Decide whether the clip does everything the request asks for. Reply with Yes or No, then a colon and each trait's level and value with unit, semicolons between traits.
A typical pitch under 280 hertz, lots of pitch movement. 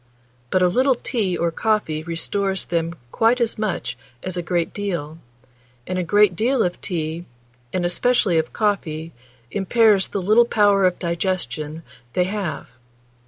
No: medium, 185 Hz; average, 3.8 semitones